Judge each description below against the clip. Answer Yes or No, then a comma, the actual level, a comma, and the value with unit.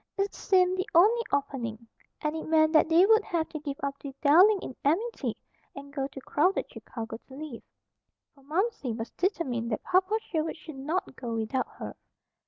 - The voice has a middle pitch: No, very high, 310 Hz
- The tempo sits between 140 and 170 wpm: No, average, 185 wpm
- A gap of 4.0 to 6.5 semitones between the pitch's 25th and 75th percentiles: Yes, wide, 5.5 semitones